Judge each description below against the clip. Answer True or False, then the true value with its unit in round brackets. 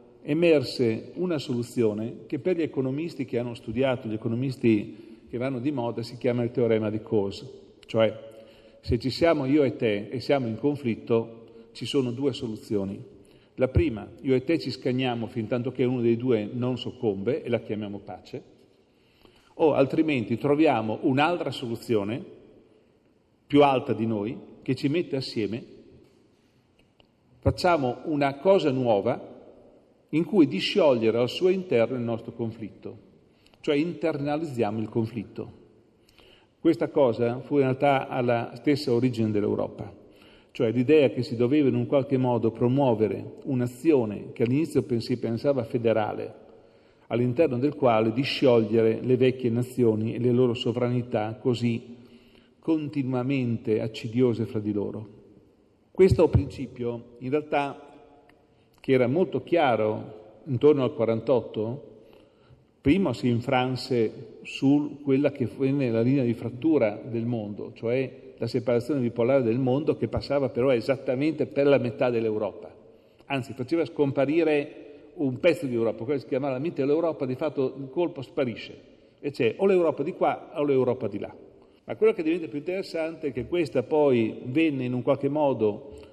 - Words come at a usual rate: True (145 wpm)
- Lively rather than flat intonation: False (3.8 semitones)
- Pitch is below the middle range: True (125 Hz)